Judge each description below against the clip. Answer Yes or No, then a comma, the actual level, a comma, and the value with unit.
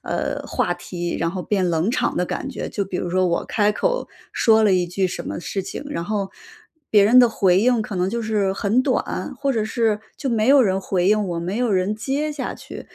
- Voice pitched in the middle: No, high, 205 Hz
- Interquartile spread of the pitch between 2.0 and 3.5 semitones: No, average, 4.0 semitones